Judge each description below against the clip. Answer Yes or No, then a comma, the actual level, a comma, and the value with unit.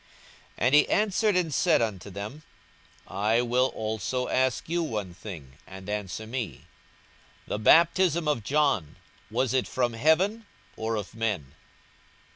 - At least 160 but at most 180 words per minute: No, average, 145 wpm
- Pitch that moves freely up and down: Yes, wide, 6.6 semitones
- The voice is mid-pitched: No, low, 115 Hz